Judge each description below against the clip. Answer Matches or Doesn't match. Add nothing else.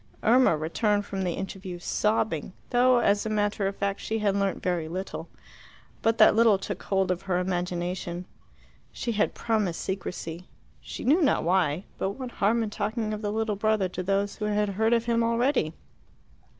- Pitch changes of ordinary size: Matches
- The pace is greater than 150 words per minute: Matches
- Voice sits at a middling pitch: Doesn't match